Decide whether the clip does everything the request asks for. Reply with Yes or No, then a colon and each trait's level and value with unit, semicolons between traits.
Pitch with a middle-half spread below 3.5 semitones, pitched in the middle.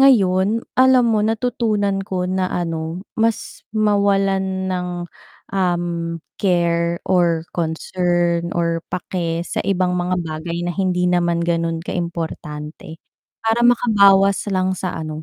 Yes: narrow, 2.6 semitones; medium, 180 Hz